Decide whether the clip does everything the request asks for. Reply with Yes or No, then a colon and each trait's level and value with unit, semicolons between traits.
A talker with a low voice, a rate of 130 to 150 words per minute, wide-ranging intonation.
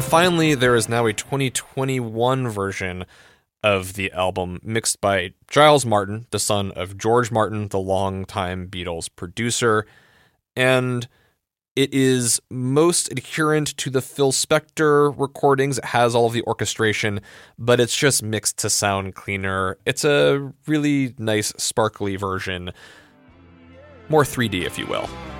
Yes: low, 110 Hz; slow, 135 wpm; wide, 5.7 semitones